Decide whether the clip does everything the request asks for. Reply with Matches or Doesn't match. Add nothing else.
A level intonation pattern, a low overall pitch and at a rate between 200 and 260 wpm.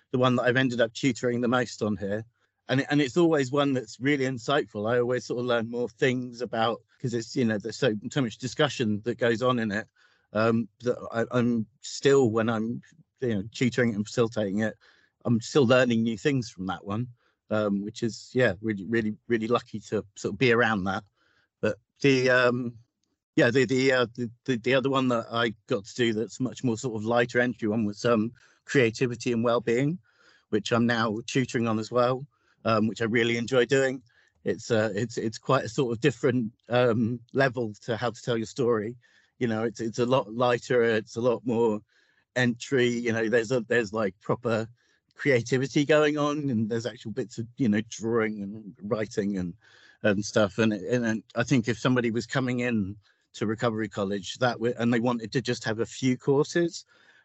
Matches